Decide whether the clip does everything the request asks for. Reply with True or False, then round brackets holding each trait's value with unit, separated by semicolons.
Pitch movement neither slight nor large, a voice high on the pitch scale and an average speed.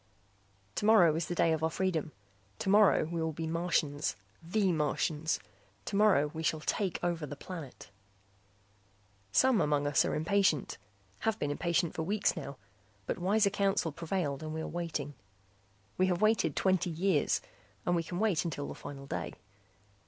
False (3.7 semitones; 170 Hz; 160 wpm)